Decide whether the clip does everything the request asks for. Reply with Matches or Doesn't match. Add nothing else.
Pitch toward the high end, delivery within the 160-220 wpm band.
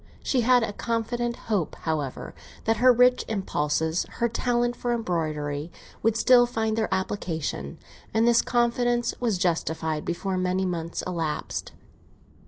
Doesn't match